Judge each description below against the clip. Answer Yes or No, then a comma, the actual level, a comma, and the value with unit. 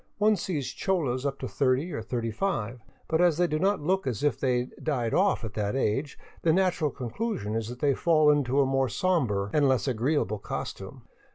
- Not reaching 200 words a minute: No, fast, 205 wpm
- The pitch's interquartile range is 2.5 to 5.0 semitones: No, wide, 5.4 semitones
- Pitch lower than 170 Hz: Yes, medium, 140 Hz